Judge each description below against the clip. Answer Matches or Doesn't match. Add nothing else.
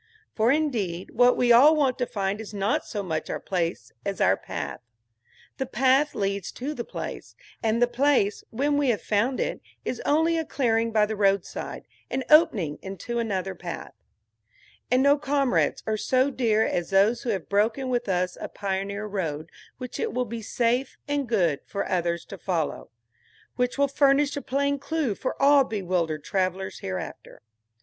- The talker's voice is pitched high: Matches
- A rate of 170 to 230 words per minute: Matches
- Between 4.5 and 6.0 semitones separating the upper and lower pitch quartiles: Matches